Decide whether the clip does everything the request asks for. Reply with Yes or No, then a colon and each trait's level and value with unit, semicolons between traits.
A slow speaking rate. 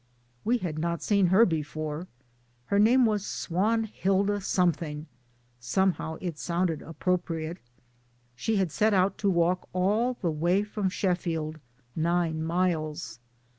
Yes: slow, 130 wpm